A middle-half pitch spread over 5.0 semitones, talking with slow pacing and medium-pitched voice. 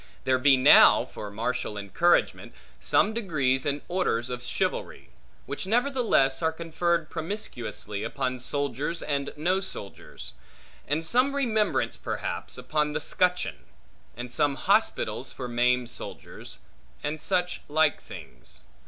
Yes: wide, 5.5 semitones; slow, 125 wpm; medium, 150 Hz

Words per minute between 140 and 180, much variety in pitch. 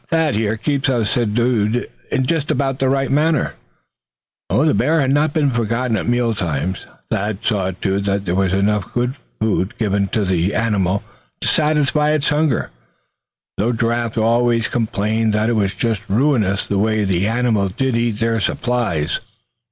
No: average, 160 wpm; average, 4.2 semitones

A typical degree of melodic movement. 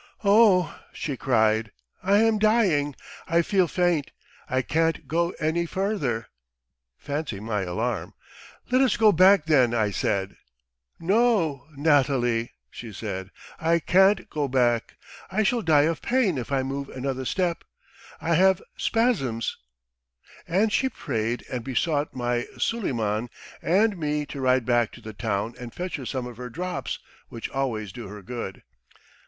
No: wide, 7.3 semitones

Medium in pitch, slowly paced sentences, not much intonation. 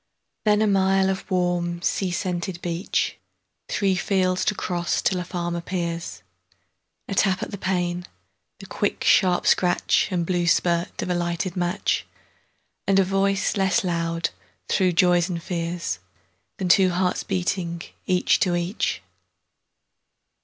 Yes: medium, 180 Hz; slow, 130 wpm; narrow, 1.7 semitones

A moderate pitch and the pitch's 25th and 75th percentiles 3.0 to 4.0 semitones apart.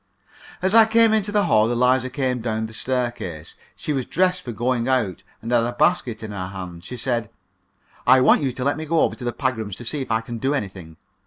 No: low, 125 Hz; average, 3.7 semitones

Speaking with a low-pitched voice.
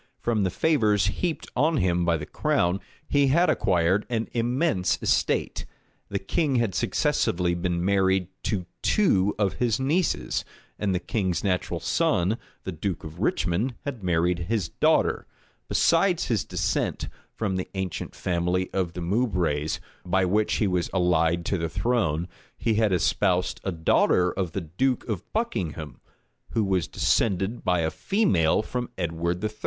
Yes: very low, 95 Hz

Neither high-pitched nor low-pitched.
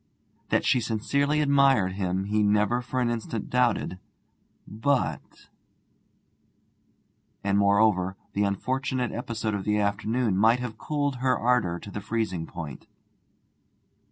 No: low, 110 Hz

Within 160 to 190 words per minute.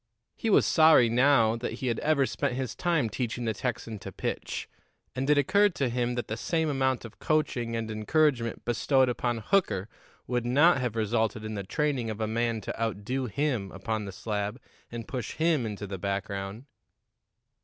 Yes: average, 185 wpm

